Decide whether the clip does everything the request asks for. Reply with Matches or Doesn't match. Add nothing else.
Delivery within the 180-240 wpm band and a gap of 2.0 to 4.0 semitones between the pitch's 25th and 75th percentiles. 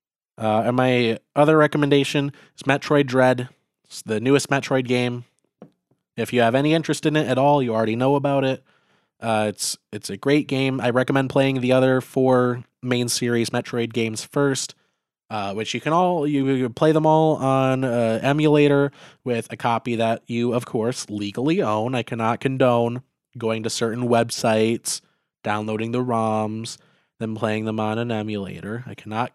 Doesn't match